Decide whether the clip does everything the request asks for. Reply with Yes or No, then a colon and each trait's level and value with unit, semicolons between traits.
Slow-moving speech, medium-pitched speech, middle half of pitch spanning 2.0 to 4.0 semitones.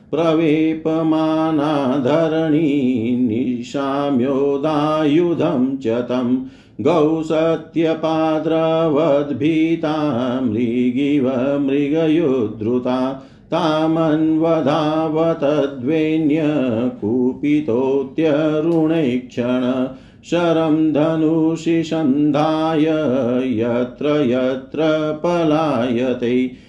Yes: slow, 35 wpm; medium, 150 Hz; average, 3.7 semitones